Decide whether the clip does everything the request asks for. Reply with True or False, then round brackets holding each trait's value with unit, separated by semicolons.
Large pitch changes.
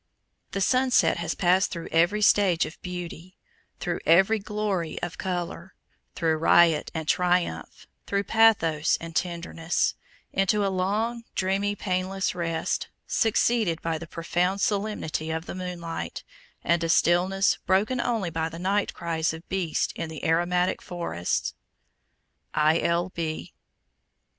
False (2.9 semitones)